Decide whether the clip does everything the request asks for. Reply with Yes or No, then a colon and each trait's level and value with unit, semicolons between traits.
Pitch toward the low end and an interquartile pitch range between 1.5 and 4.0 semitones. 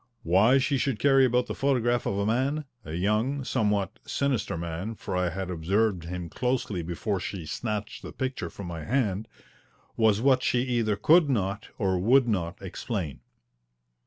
No: low, 105 Hz; wide, 5.4 semitones